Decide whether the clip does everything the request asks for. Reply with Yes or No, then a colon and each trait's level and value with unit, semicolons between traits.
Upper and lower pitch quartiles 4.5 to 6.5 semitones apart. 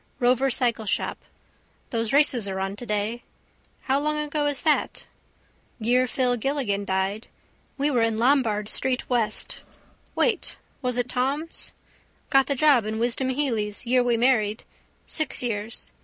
No: average, 3.7 semitones